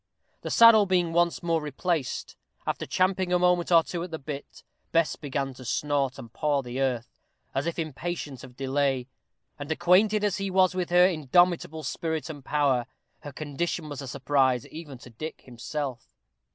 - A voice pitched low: No, medium, 155 Hz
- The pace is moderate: Yes, average, 175 wpm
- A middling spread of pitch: Yes, average, 4.5 semitones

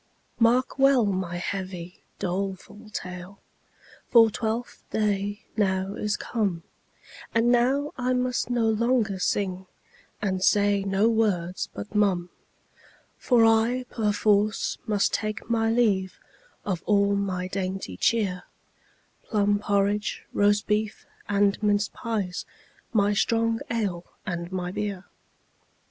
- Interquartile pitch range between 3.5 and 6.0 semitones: No, average, 2.9 semitones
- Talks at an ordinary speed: No, slow, 115 wpm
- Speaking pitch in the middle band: No, high, 205 Hz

